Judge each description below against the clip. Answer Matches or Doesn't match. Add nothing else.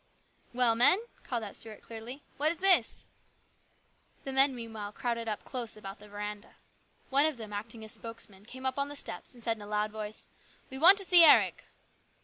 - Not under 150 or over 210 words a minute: Matches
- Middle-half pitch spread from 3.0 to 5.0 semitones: Matches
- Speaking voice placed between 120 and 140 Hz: Doesn't match